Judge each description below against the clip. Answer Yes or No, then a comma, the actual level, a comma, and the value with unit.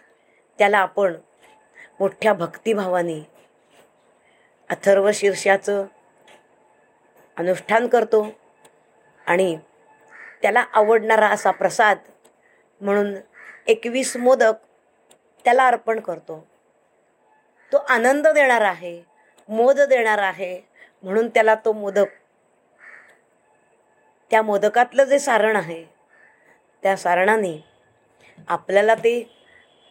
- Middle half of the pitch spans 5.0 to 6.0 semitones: No, average, 3.3 semitones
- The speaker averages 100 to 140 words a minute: No, slow, 80 wpm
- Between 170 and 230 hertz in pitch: Yes, high, 210 Hz